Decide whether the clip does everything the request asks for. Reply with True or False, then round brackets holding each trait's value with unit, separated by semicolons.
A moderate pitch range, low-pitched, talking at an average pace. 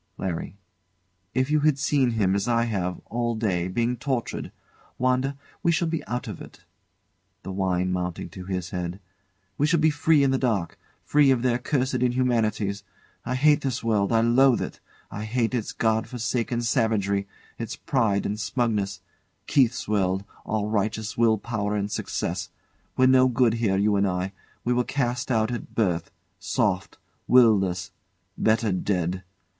True (4.3 semitones; 115 Hz; 165 wpm)